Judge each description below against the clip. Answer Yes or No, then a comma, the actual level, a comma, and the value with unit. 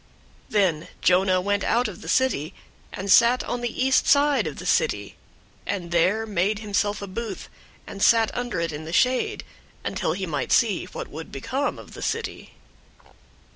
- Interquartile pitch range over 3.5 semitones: Yes, average, 4.8 semitones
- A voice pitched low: No, high, 205 Hz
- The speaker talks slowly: No, average, 175 wpm